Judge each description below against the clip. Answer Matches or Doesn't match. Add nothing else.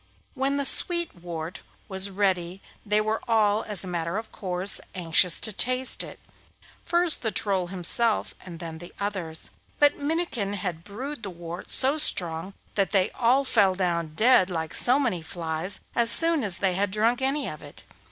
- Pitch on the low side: Doesn't match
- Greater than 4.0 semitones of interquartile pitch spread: Matches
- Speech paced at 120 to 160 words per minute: Doesn't match